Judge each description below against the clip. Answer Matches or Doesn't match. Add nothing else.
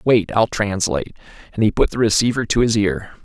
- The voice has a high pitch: Doesn't match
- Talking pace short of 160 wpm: Doesn't match